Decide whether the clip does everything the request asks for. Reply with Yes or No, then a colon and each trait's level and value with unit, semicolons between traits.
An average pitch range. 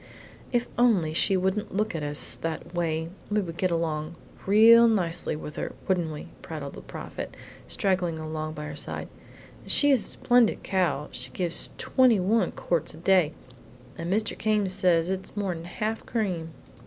Yes: average, 4.6 semitones